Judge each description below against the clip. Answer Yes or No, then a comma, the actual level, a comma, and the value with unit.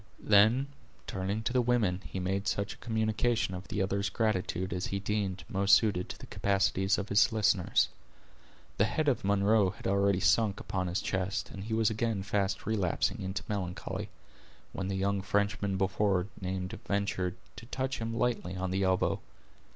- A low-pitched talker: Yes, low, 100 Hz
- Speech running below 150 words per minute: No, average, 175 wpm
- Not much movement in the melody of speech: Yes, narrow, 2.3 semitones